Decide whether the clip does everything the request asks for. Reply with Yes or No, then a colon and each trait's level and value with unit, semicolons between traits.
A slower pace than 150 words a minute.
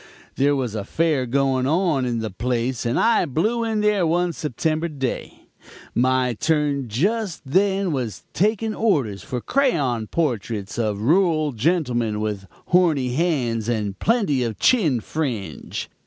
Yes: average, 140 wpm